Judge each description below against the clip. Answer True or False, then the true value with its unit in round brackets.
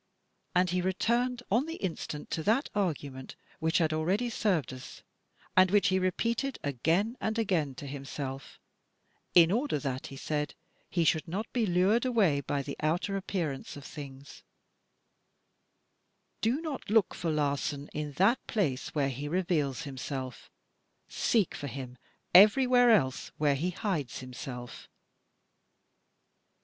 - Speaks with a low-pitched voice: False (165 Hz)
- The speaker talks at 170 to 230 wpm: False (140 wpm)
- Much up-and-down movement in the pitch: True (6.7 semitones)